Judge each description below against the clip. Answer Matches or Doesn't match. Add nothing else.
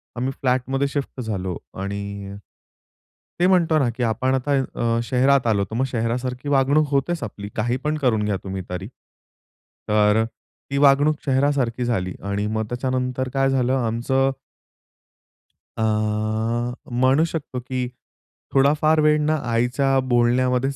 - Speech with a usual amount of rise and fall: Matches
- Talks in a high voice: Doesn't match